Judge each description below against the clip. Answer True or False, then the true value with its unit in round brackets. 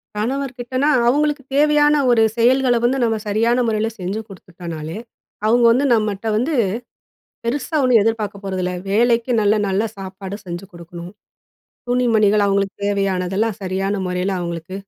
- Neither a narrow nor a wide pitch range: True (4.3 semitones)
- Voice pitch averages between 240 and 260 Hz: False (215 Hz)